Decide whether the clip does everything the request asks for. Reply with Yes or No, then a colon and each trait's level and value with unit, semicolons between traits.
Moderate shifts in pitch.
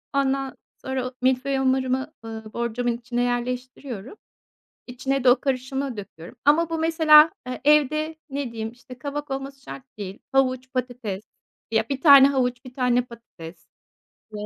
No: narrow, 2.3 semitones